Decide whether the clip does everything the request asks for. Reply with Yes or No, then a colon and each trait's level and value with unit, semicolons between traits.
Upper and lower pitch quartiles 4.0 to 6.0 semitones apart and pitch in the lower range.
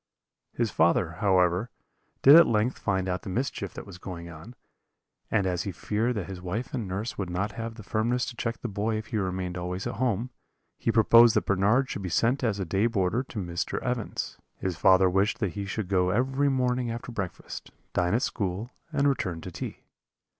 Yes: average, 4.3 semitones; low, 100 Hz